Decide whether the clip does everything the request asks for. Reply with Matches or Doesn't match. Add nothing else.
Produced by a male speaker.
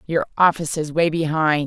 Doesn't match